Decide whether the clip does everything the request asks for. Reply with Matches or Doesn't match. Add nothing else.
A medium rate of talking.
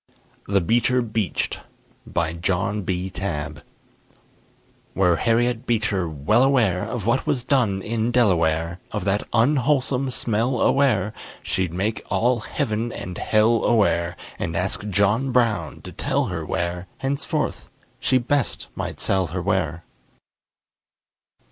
Doesn't match